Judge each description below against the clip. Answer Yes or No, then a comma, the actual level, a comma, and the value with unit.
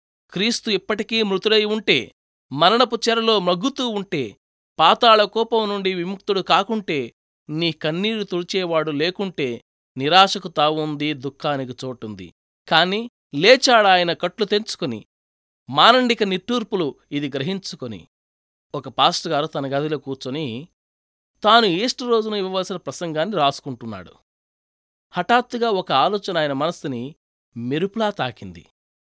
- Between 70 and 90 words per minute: No, average, 100 wpm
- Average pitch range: No, wide, 7.4 semitones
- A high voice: No, medium, 175 Hz